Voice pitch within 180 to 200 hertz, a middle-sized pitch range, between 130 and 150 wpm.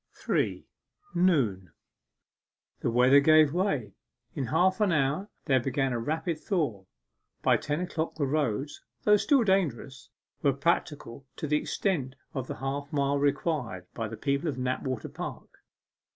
No: medium, 140 Hz; average, 3.8 semitones; average, 145 wpm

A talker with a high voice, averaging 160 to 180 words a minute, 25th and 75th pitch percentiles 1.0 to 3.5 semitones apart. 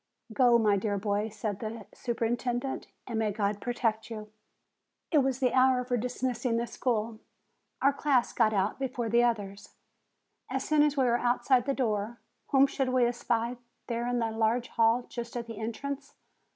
Yes: high, 235 Hz; average, 175 wpm; narrow, 2.5 semitones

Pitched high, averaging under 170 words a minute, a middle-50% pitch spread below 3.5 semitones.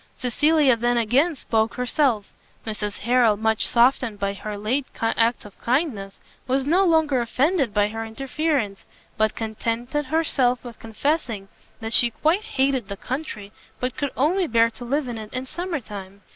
No: high, 245 Hz; average, 160 wpm; average, 4.4 semitones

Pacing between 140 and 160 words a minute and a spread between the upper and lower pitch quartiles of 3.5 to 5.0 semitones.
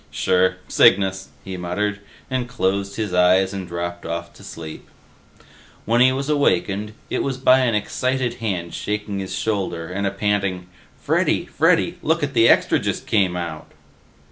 Yes: average, 155 wpm; average, 4.1 semitones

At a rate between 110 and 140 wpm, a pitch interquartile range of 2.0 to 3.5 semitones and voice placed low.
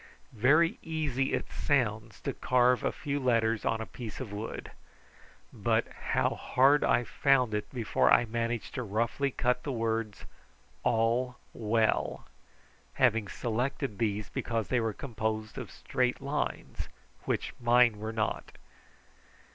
Yes: slow, 135 wpm; narrow, 2.5 semitones; low, 120 Hz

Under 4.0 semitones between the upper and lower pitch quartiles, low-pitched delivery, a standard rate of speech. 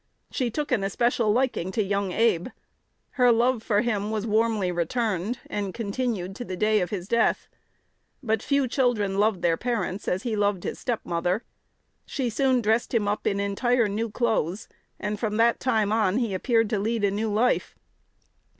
No: average, 3.0 semitones; high, 215 Hz; average, 180 wpm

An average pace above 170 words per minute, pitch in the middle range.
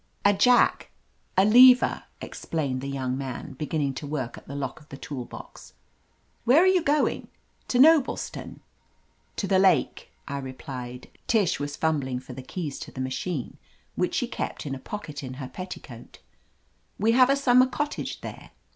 Yes: average, 180 wpm; medium, 150 Hz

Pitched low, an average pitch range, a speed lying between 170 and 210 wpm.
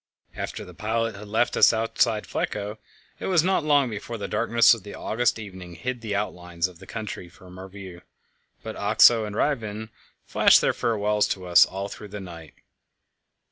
Yes: low, 105 Hz; average, 3.3 semitones; average, 180 wpm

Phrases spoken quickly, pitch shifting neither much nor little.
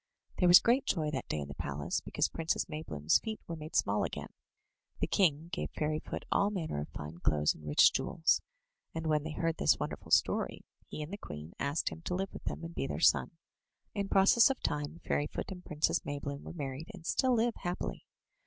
Yes: fast, 210 wpm; average, 4.2 semitones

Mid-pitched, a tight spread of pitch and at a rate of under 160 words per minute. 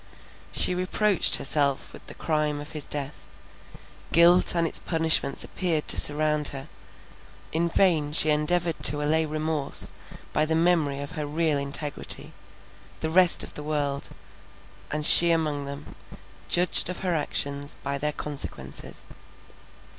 Yes: medium, 150 Hz; narrow, 2.3 semitones; average, 140 wpm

